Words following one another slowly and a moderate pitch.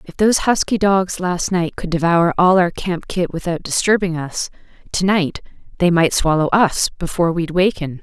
No: average, 180 wpm; medium, 175 Hz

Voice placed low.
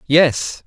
No: medium, 145 Hz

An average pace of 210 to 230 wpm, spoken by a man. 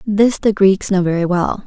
No: fast, 215 wpm; female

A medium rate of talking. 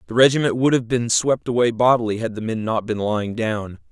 No: fast, 230 wpm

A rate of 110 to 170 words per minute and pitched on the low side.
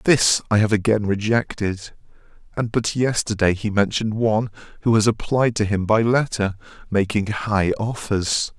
Yes: average, 145 wpm; low, 105 Hz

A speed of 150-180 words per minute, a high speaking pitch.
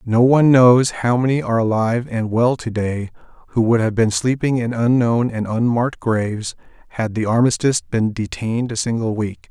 No: average, 175 wpm; low, 115 Hz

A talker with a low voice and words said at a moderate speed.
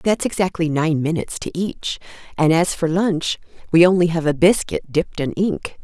No: medium, 170 Hz; average, 185 wpm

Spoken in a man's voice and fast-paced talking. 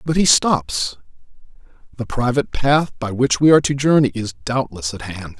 No: male; average, 180 wpm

